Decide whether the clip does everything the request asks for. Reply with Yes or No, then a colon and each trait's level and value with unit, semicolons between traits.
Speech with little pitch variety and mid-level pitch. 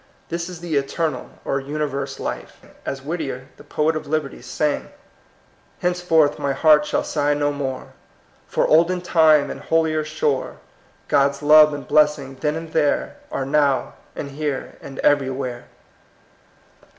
Yes: narrow, 2.2 semitones; medium, 150 Hz